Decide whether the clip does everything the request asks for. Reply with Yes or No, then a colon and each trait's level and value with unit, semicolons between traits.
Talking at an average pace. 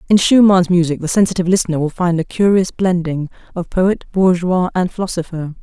Yes: average, 170 wpm